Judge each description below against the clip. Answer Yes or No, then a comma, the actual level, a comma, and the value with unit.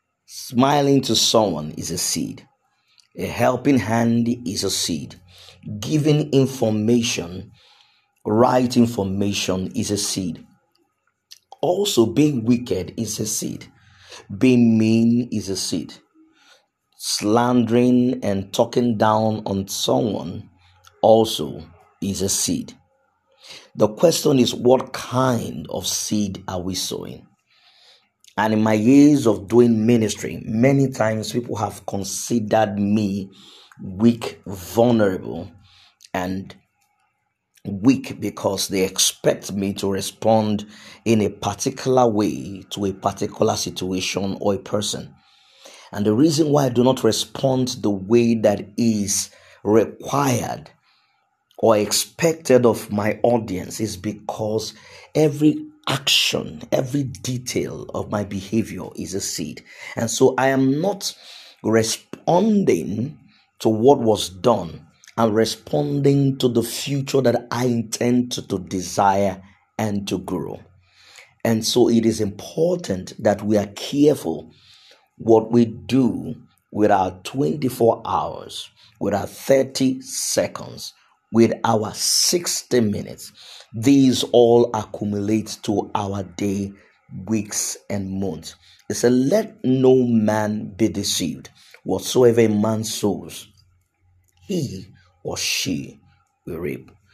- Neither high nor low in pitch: No, low, 110 Hz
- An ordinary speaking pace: No, slow, 115 wpm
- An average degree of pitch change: Yes, average, 3.8 semitones